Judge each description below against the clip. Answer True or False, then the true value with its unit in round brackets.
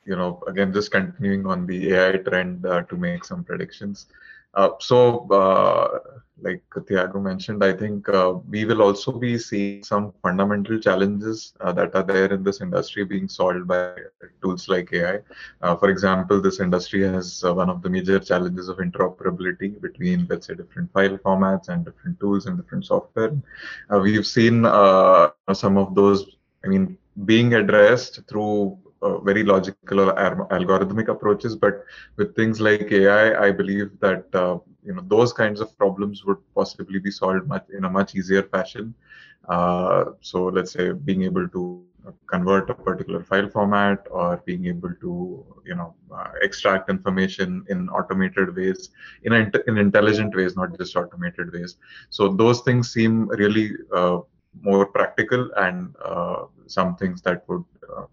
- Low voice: True (100 Hz)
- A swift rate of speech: False (165 wpm)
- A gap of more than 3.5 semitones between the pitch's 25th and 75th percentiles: False (2.9 semitones)